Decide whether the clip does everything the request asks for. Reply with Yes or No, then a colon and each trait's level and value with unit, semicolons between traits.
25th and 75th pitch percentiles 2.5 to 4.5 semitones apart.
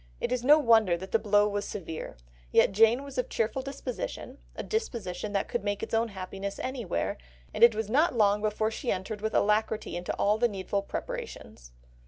Yes: average, 3.1 semitones